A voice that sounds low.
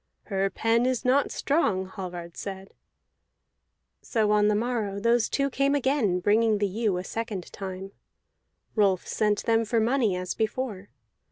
No: high, 210 Hz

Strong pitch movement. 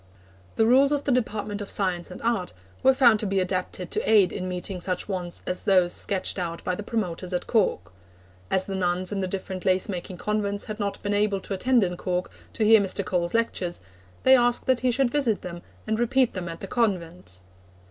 No: average, 3.5 semitones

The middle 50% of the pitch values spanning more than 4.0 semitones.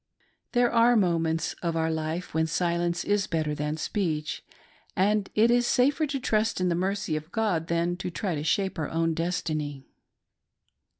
Yes: average, 4.5 semitones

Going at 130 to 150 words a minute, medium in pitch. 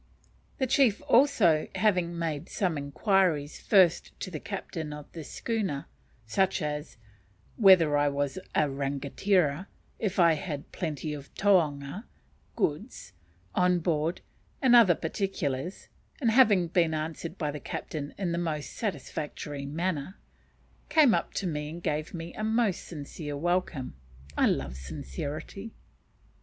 Yes: slow, 135 wpm; medium, 165 Hz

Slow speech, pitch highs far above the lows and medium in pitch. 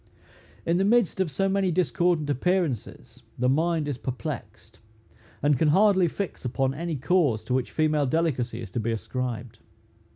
No: average, 160 wpm; wide, 5.8 semitones; medium, 150 Hz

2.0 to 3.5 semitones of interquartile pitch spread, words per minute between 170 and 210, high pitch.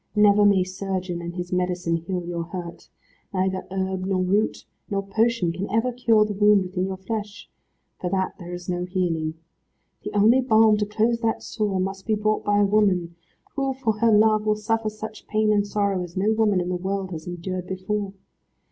Yes: average, 2.8 semitones; average, 195 wpm; high, 195 Hz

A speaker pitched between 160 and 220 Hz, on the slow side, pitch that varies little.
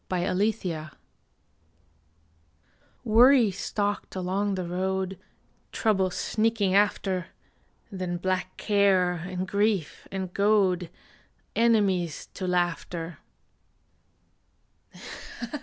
Yes: high, 190 Hz; slow, 75 wpm; narrow, 2.2 semitones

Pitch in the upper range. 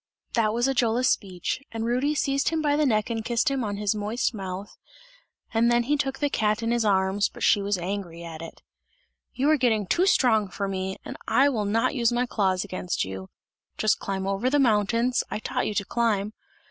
Yes: high, 220 Hz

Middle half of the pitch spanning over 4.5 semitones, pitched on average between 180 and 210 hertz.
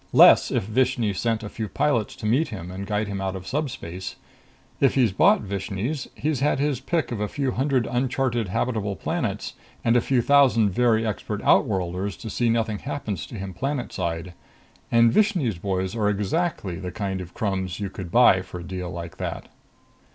No: average, 4.9 semitones; low, 110 Hz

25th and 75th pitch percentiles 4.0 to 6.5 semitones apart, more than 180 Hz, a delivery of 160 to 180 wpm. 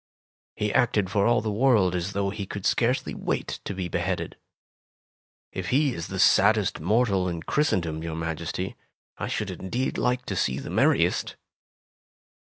No: average, 4.6 semitones; low, 100 Hz; average, 165 wpm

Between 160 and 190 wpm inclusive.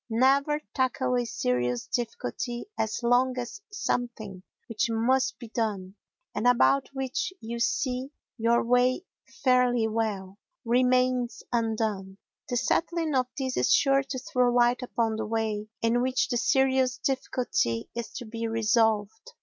No: average, 140 wpm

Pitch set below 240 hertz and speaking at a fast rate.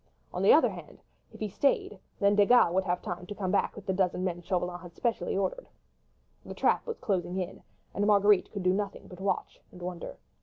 Yes: high, 190 Hz; fast, 220 wpm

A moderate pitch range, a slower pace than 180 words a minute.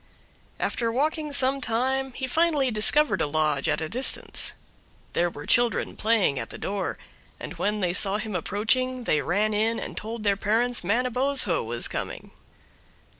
Yes: average, 4.8 semitones; average, 160 wpm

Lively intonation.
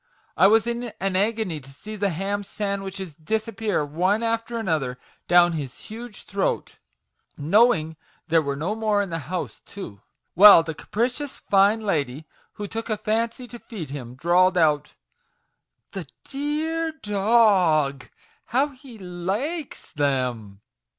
Yes: wide, 5.9 semitones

